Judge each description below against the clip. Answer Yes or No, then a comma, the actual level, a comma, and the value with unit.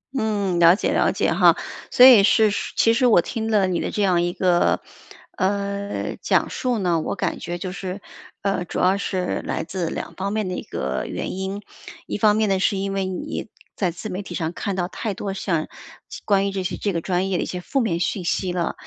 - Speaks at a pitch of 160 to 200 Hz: Yes, high, 190 Hz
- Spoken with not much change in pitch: Yes, narrow, 2.3 semitones